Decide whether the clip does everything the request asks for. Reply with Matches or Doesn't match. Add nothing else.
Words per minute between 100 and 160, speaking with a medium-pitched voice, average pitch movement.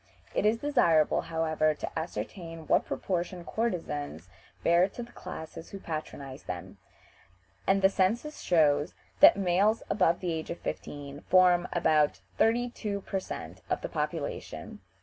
Matches